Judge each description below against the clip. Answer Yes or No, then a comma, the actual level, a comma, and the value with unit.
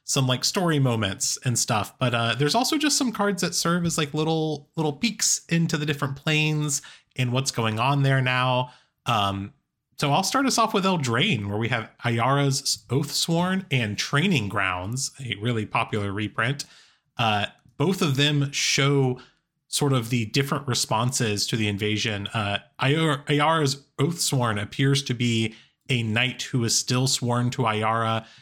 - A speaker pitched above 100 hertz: Yes, low, 135 Hz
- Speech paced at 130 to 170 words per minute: Yes, average, 165 wpm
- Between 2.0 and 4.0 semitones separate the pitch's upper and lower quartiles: No, average, 4.5 semitones